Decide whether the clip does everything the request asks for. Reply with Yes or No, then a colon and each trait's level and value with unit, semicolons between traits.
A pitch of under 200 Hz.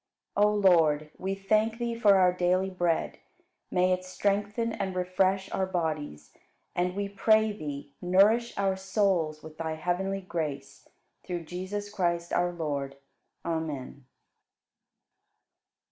Yes: medium, 185 Hz